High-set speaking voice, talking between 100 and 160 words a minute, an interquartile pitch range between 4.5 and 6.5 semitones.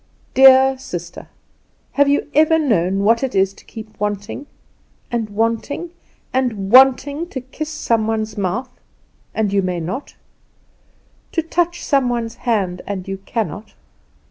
Yes: high, 230 Hz; average, 140 wpm; average, 5.1 semitones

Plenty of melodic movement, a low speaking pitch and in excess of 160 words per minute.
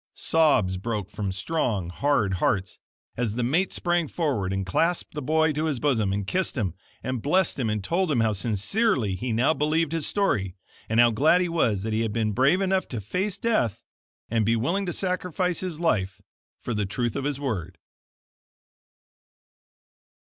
Yes: wide, 7.8 semitones; low, 125 Hz; average, 180 wpm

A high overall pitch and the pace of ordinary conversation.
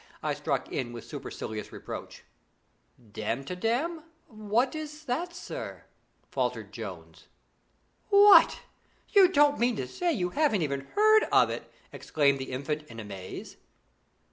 No: high, 220 Hz; slow, 125 wpm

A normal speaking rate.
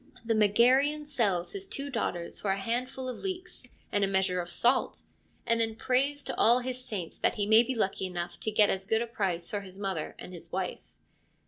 No: fast, 215 wpm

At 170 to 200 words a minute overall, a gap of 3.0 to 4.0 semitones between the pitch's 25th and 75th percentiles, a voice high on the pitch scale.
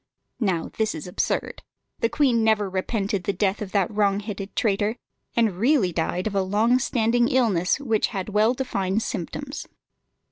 No: average, 155 wpm; average, 3.3 semitones; high, 210 Hz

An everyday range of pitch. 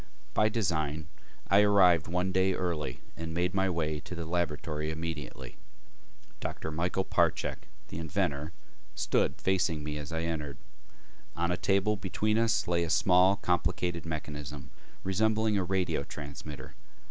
Yes: average, 3.6 semitones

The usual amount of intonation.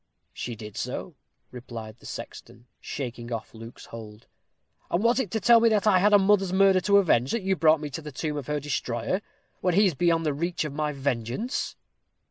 No: wide, 8.2 semitones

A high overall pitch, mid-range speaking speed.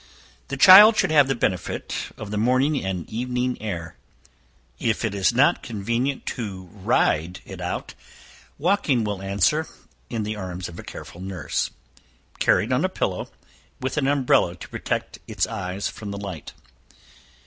No: low, 110 Hz; average, 155 wpm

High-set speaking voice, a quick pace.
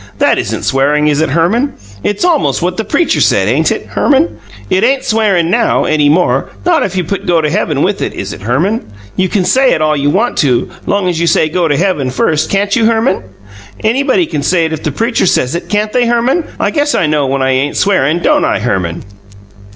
No: medium, 180 Hz; fast, 230 wpm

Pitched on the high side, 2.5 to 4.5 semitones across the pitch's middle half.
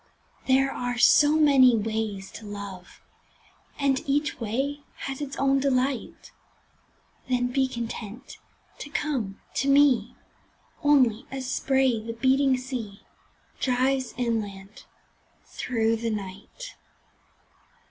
Yes: very high, 255 Hz; average, 3.5 semitones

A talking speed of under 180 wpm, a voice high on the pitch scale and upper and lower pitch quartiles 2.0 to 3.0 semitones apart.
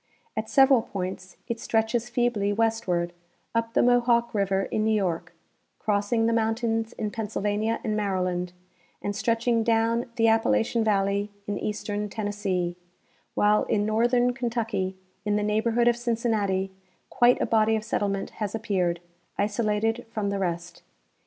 Yes: average, 140 wpm; high, 215 Hz; narrow, 2.4 semitones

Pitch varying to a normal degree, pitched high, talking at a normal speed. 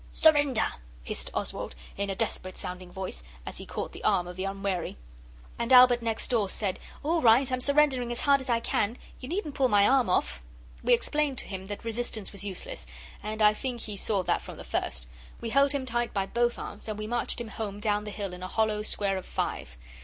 No: average, 4.2 semitones; high, 220 Hz; fast, 220 wpm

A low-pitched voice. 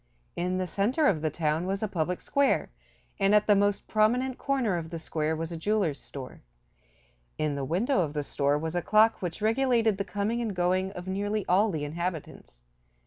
No: medium, 185 Hz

